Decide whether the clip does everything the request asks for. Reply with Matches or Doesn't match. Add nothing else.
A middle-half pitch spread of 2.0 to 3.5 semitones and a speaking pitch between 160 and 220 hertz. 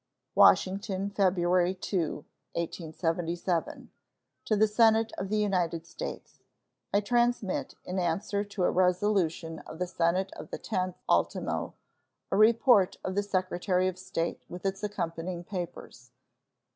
Matches